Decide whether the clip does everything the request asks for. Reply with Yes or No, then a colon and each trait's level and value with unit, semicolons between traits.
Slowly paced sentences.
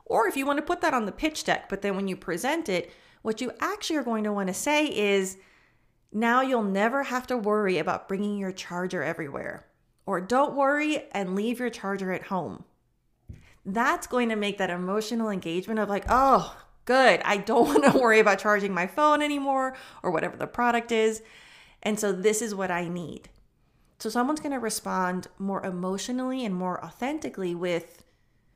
No: average, 190 wpm